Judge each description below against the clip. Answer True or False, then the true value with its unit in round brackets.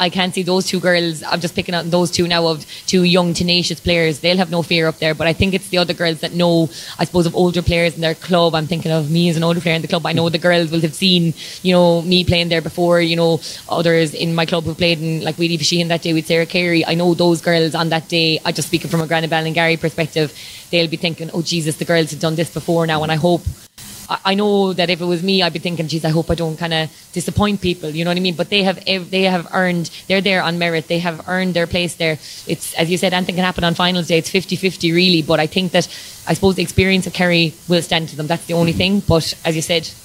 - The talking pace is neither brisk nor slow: False (285 wpm)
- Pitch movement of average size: False (1.4 semitones)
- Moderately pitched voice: True (170 Hz)